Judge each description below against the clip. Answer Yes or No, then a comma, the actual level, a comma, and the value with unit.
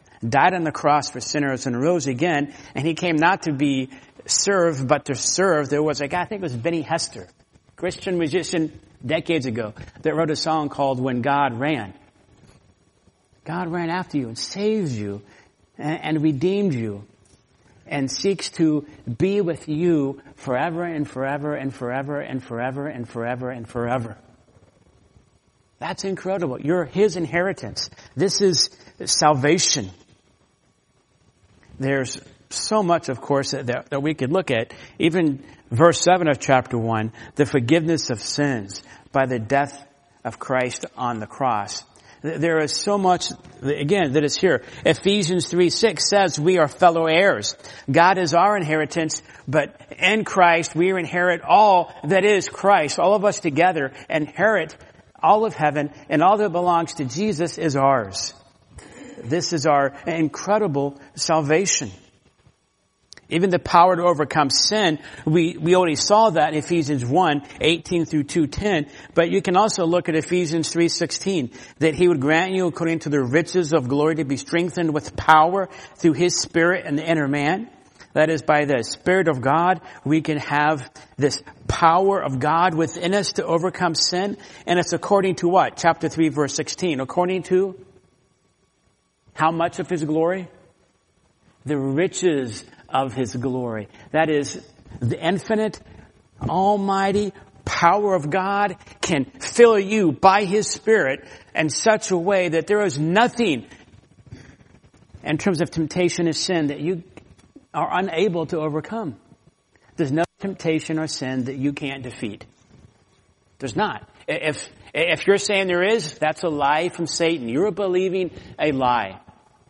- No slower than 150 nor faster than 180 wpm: Yes, average, 155 wpm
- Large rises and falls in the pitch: No, average, 4.7 semitones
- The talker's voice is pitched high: No, medium, 155 Hz